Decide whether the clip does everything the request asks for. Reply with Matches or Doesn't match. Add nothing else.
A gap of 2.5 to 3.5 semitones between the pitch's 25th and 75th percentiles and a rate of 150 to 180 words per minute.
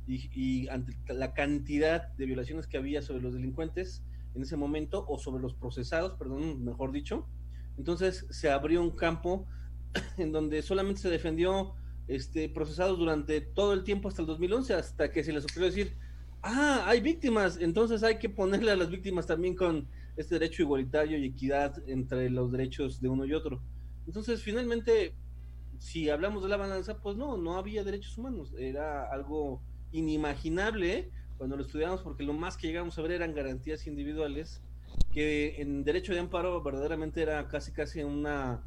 Doesn't match